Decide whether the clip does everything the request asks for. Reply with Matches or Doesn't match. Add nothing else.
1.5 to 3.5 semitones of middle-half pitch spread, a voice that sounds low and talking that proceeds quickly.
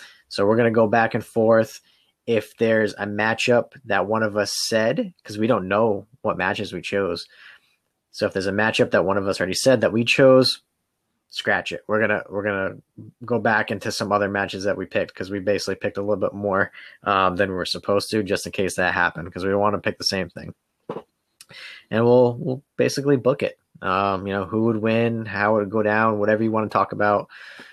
Matches